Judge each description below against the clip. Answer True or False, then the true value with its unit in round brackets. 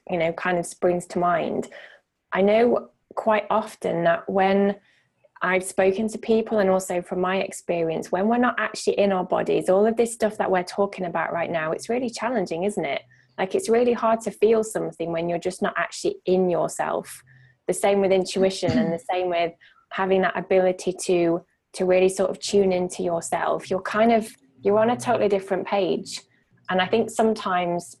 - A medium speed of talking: True (195 wpm)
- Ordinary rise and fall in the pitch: True (3.1 semitones)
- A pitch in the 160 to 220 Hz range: True (190 Hz)